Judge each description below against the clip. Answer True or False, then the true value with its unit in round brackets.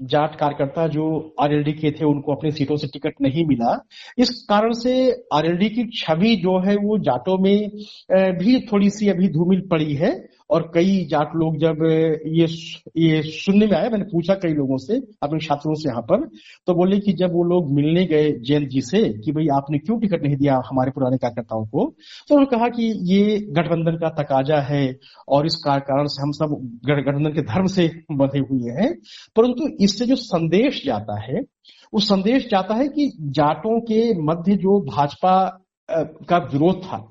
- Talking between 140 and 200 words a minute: True (185 wpm)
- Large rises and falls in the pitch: True (5.8 semitones)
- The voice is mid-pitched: True (165 Hz)